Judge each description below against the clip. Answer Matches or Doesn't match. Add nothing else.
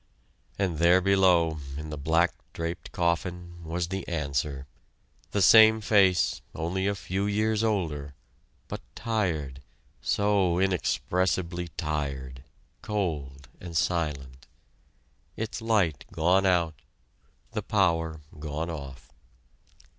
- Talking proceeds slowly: Matches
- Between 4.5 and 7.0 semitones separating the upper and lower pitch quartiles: Doesn't match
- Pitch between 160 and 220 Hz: Doesn't match